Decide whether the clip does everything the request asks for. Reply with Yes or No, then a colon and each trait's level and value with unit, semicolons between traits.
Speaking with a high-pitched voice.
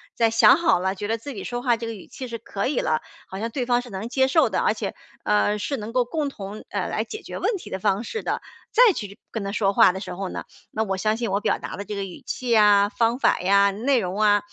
Yes: high, 215 Hz